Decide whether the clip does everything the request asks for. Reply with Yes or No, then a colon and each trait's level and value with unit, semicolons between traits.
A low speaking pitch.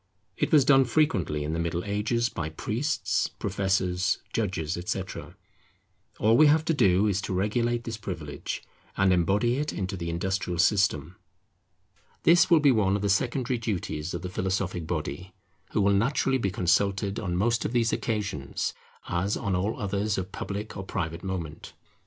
Yes: low, 100 Hz